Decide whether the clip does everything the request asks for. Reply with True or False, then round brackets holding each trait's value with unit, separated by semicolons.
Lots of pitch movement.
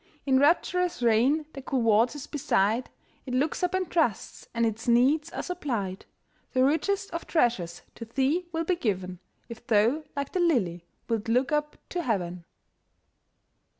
True (6.2 semitones)